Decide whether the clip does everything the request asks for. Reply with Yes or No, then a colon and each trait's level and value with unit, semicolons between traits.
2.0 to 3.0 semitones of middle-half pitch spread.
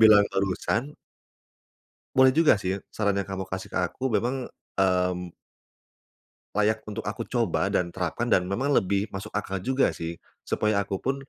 No: average, 3.6 semitones